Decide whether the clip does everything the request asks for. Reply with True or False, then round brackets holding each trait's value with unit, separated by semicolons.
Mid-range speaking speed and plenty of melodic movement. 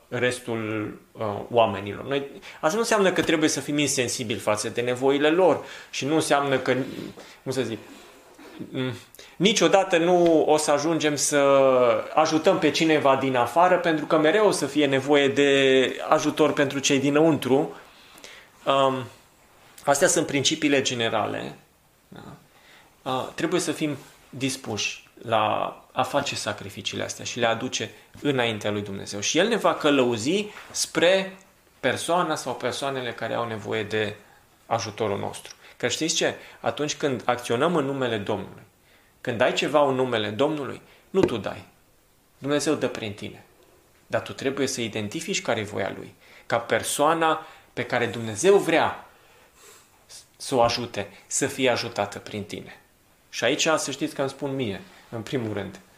False (150 wpm; 4.5 semitones)